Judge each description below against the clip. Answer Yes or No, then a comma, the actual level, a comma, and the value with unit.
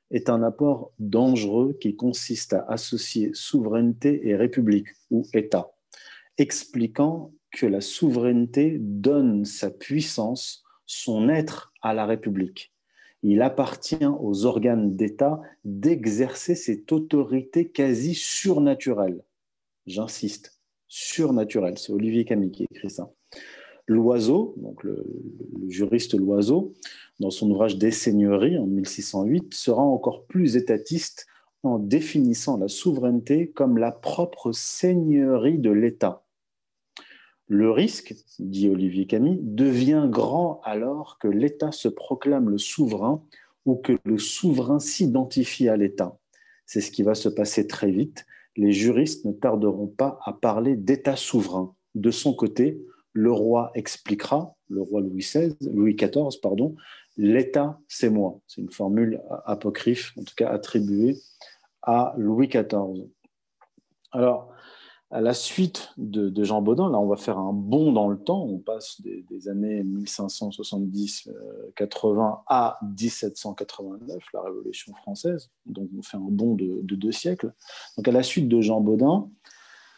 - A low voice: Yes, low, 115 Hz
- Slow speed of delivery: Yes, slow, 130 wpm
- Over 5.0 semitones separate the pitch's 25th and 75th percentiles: Yes, wide, 5.5 semitones